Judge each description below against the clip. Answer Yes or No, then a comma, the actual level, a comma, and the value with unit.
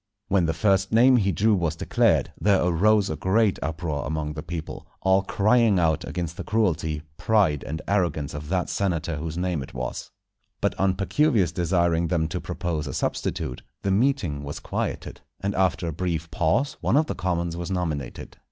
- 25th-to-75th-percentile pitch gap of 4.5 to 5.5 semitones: No, average, 3.7 semitones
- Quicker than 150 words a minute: Yes, average, 180 wpm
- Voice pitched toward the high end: No, very low, 90 Hz